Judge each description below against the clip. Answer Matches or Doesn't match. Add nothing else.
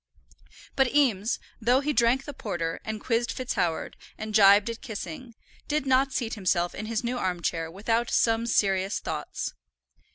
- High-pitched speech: Matches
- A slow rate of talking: Doesn't match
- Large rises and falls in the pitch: Doesn't match